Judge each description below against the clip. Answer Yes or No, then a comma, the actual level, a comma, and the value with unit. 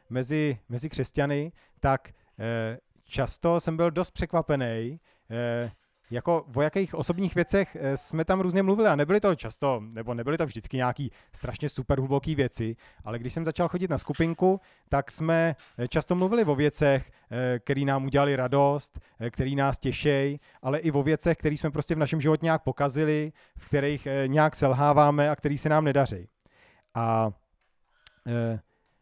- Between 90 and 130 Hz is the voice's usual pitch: No, medium, 140 Hz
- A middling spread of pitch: Yes, average, 4.1 semitones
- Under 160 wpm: No, average, 165 wpm